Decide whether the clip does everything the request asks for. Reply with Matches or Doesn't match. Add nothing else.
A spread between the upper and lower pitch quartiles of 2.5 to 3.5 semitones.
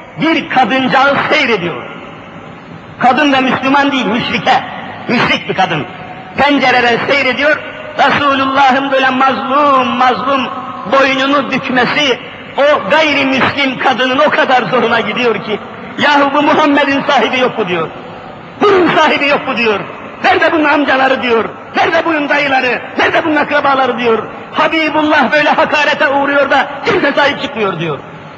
Matches